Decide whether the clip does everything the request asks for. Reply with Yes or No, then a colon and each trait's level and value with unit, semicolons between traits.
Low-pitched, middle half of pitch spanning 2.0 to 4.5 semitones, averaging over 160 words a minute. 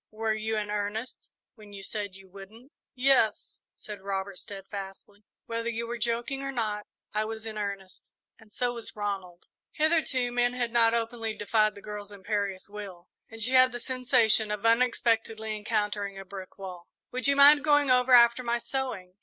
No: high, 220 Hz; average, 3.0 semitones; average, 175 wpm